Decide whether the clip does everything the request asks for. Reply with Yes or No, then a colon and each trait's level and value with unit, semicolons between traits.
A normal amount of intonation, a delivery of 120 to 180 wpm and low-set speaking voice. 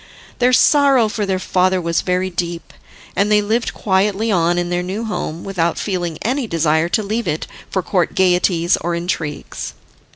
No: average, 3.5 semitones; average, 170 wpm; medium, 185 Hz